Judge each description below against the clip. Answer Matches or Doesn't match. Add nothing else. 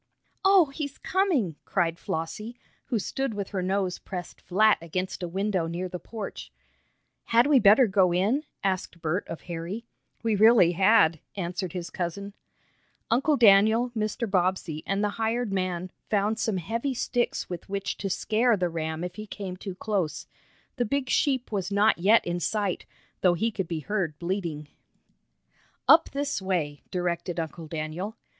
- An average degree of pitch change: Matches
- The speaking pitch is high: Matches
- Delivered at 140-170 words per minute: Matches